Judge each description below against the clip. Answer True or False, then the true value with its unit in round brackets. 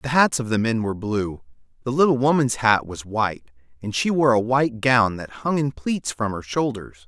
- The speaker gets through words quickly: True (220 wpm)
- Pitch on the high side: False (120 Hz)